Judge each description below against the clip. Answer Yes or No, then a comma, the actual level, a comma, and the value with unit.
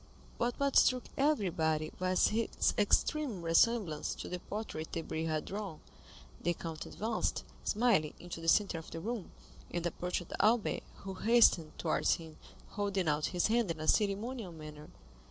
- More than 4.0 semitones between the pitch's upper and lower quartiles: Yes, average, 5.3 semitones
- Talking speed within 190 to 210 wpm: No, average, 155 wpm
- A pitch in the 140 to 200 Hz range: Yes, medium, 185 Hz